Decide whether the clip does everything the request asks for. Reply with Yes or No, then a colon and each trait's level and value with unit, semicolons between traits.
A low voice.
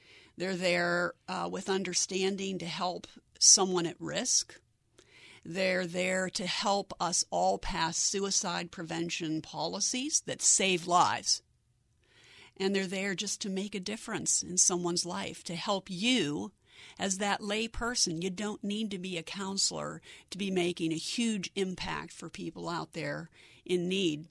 No: medium, 185 Hz